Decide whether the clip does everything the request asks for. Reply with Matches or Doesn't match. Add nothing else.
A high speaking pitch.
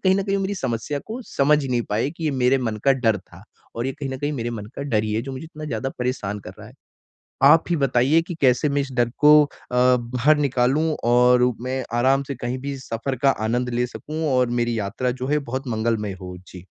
Doesn't match